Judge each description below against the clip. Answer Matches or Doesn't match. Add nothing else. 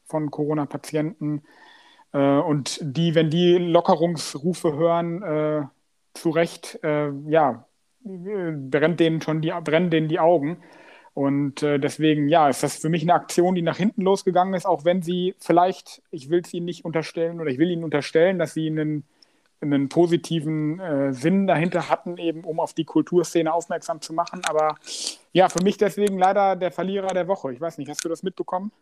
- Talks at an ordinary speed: Matches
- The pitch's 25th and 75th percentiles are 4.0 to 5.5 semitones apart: Doesn't match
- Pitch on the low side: Doesn't match